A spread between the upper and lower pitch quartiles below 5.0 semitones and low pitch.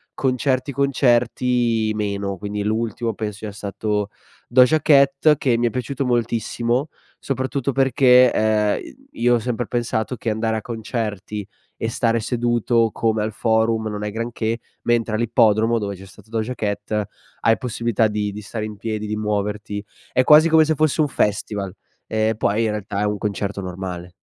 Yes: average, 2.7 semitones; low, 110 Hz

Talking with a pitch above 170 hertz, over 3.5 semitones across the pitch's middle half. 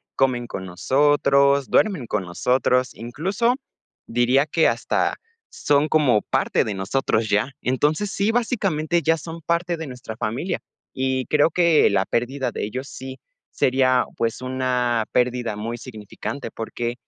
No: low, 130 Hz; average, 4.4 semitones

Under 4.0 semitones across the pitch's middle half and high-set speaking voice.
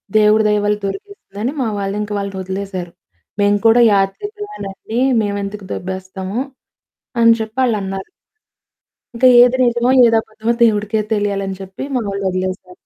Yes: average, 2.9 semitones; high, 205 Hz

